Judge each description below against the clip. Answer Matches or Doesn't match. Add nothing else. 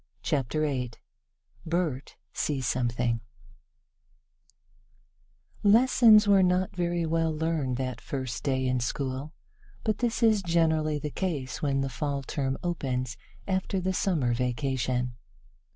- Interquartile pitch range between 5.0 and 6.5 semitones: Matches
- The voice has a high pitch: Doesn't match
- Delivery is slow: Matches